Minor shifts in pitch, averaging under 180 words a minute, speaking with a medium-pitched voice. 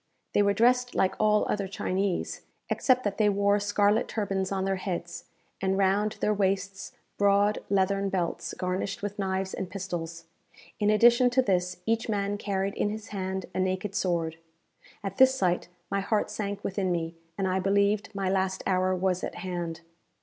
No: narrow, 1.7 semitones; average, 170 wpm; high, 195 Hz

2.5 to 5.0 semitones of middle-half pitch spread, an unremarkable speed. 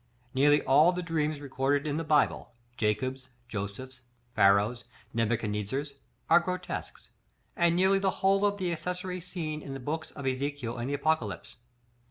No: wide, 5.5 semitones; average, 150 wpm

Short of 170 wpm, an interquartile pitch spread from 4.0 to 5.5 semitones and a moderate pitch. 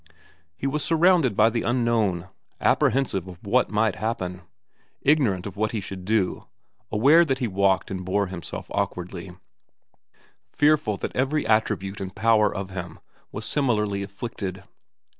No: average, 140 wpm; average, 4.3 semitones; low, 105 Hz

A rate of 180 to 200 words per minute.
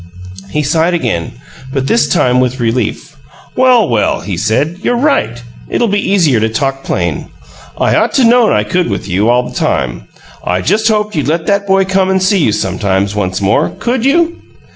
Yes: average, 190 wpm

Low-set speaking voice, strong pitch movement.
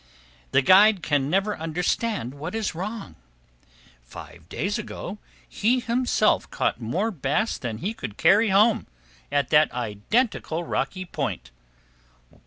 No: medium, 180 Hz; wide, 7.5 semitones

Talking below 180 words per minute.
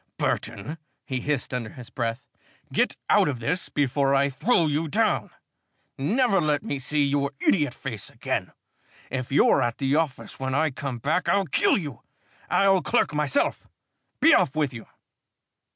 Yes: average, 160 wpm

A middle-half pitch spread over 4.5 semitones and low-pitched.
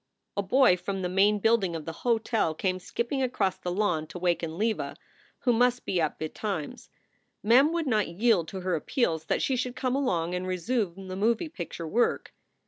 No: average, 5.2 semitones; high, 195 Hz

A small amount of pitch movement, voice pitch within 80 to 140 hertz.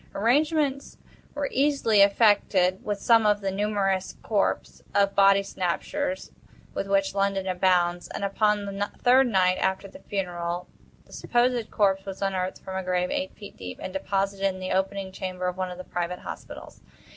No: narrow, 2.0 semitones; high, 195 Hz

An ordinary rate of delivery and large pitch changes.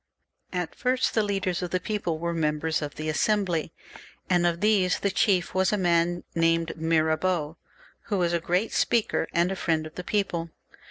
No: average, 185 wpm; average, 2.7 semitones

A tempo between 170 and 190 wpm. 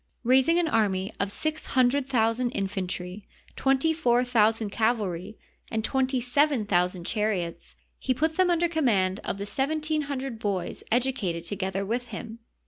No: average, 155 wpm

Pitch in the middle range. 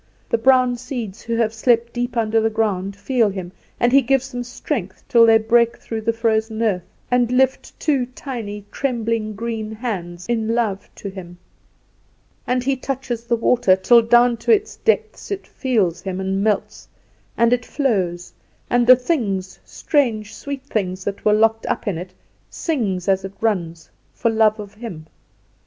No: high, 225 Hz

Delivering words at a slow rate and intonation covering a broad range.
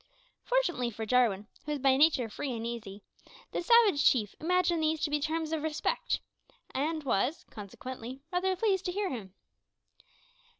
No: average, 160 wpm; wide, 6.2 semitones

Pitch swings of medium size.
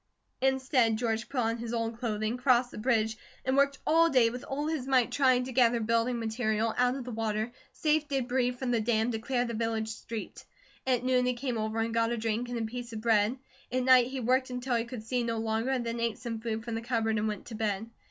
No: narrow, 2.1 semitones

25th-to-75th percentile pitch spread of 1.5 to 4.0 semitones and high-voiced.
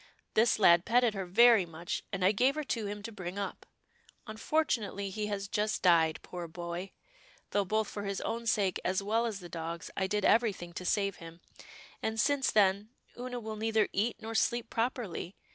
Yes: average, 3.5 semitones; high, 205 Hz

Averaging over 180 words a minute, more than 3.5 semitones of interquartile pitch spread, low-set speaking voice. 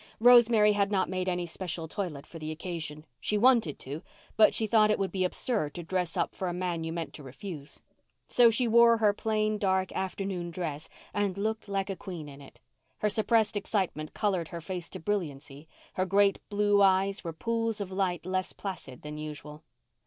No: average, 195 wpm; average, 4.2 semitones; high, 190 Hz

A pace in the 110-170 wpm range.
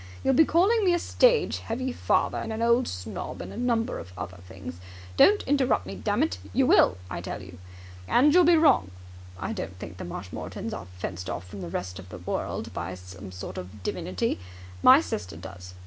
No: average, 200 wpm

